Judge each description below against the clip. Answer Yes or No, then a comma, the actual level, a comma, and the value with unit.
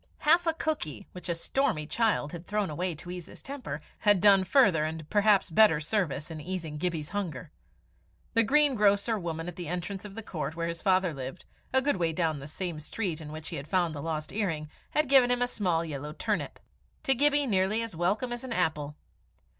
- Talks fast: Yes, fast, 210 wpm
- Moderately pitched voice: Yes, medium, 180 Hz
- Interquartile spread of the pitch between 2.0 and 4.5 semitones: No, wide, 5.6 semitones